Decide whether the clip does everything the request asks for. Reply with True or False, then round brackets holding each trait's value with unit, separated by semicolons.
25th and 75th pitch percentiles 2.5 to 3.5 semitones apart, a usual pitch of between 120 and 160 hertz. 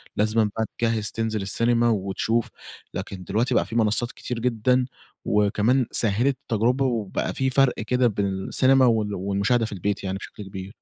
False (3.2 semitones; 110 Hz)